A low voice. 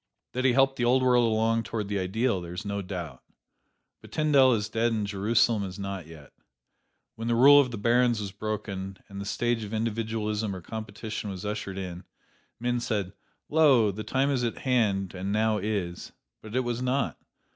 Yes: low, 110 Hz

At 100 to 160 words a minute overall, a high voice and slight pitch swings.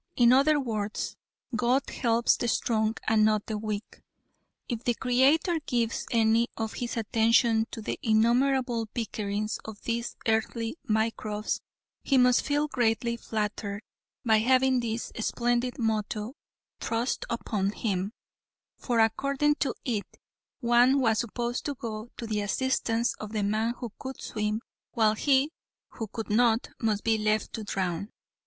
Yes: average, 145 wpm; high, 230 Hz; narrow, 2.2 semitones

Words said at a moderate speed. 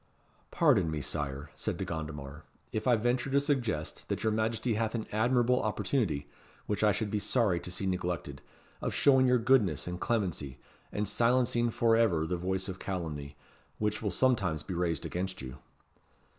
Yes: average, 170 wpm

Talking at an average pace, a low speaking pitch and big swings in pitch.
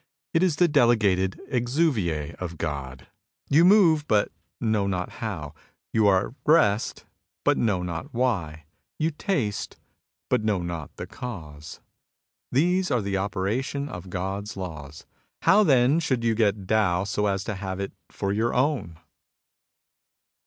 Yes: average, 145 wpm; low, 105 Hz; wide, 6.0 semitones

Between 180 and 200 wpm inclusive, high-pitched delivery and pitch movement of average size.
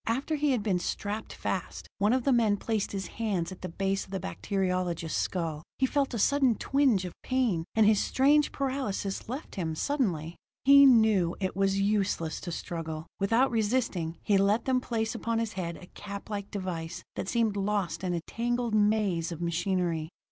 Yes: average, 185 wpm; high, 200 Hz; average, 4.7 semitones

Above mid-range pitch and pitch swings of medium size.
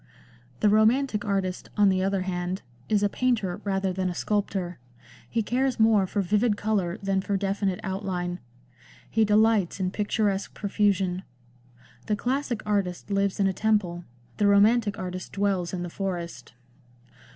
No: high, 200 Hz; narrow, 2.2 semitones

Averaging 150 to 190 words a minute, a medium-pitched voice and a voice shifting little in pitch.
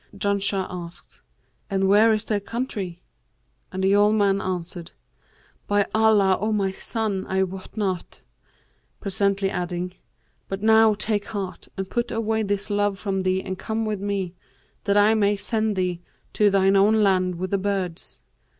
No: average, 160 wpm; high, 200 Hz; narrow, 2.0 semitones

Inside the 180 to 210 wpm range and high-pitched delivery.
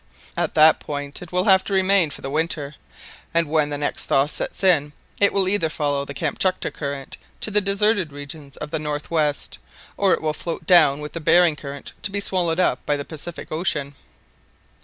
No: average, 200 wpm; medium, 155 Hz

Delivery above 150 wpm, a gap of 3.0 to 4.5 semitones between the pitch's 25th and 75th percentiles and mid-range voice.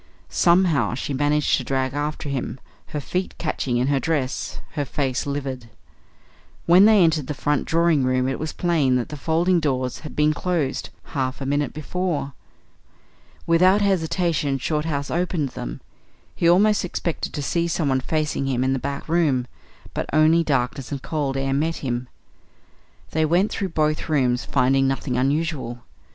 Yes: average, 160 wpm; average, 3.7 semitones; medium, 145 Hz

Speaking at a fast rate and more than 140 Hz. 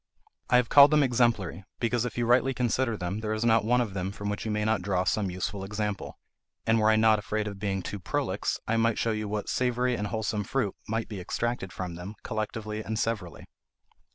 No: fast, 220 wpm; low, 110 Hz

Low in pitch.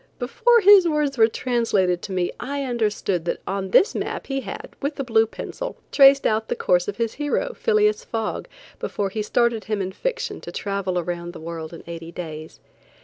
No: high, 220 Hz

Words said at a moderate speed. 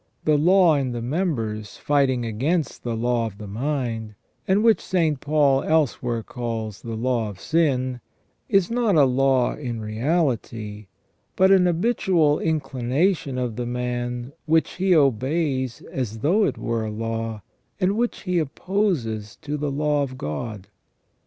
Yes: average, 150 wpm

